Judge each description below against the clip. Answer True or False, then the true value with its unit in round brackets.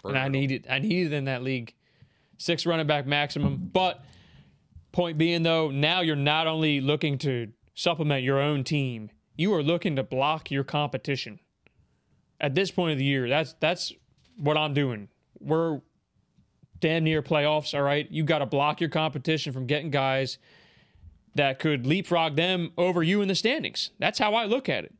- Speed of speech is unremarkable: True (180 wpm)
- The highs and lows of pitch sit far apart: False (3.2 semitones)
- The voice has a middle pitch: True (150 Hz)